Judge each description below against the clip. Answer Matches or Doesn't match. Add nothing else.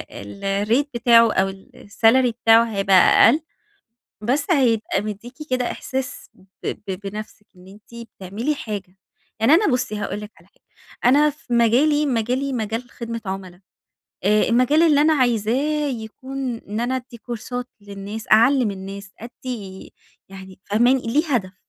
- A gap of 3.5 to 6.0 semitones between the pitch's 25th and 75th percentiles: Matches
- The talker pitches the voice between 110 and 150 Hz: Doesn't match